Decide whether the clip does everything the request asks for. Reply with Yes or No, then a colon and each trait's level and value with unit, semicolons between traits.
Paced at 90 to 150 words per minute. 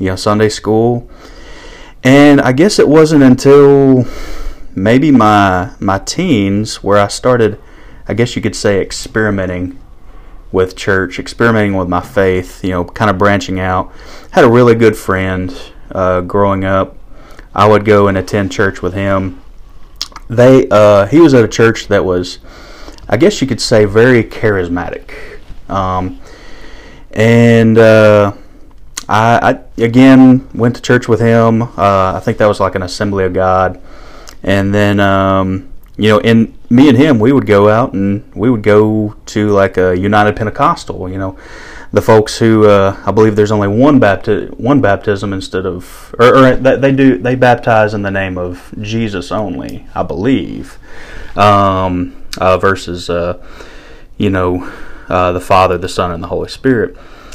No: average, 160 wpm